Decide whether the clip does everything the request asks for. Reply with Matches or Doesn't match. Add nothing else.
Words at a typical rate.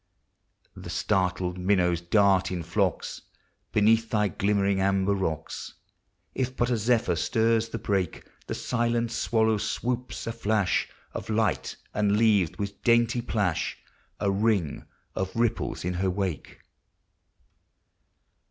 Doesn't match